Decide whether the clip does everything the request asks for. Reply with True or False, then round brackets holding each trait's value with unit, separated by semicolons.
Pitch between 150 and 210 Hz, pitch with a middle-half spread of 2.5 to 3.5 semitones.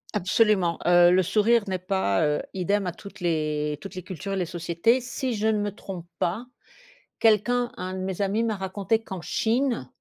False (190 Hz; 3.9 semitones)